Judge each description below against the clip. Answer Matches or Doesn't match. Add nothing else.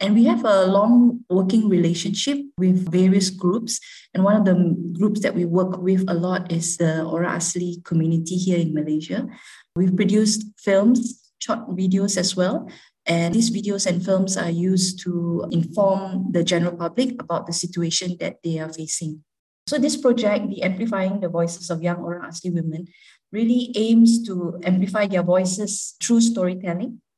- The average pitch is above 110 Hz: Matches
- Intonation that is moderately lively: Matches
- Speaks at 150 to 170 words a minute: Matches